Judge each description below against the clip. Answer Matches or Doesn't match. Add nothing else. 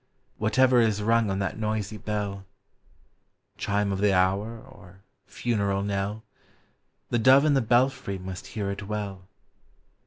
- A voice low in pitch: Matches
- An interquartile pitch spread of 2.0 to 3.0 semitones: Matches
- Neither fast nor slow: Matches